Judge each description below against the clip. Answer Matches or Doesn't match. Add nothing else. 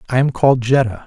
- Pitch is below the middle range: Matches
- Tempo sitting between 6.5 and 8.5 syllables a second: Matches